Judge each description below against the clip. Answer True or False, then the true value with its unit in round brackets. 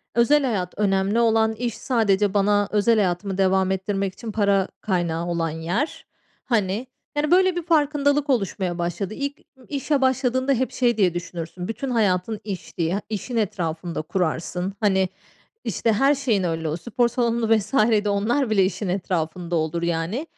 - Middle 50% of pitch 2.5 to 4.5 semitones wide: False (5.0 semitones)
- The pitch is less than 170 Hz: False (205 Hz)